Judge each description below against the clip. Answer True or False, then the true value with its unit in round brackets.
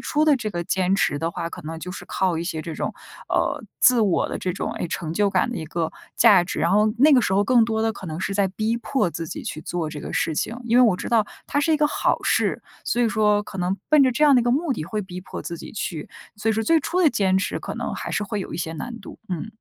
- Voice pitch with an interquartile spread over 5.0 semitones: True (5.4 semitones)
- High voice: True (205 Hz)